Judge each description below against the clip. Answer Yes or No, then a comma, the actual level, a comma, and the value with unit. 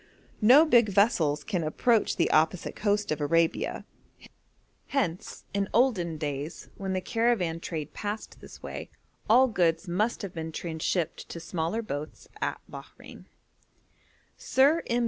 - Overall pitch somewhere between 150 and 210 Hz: Yes, medium, 185 Hz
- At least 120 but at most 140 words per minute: Yes, slow, 135 wpm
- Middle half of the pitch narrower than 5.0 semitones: No, wide, 5.6 semitones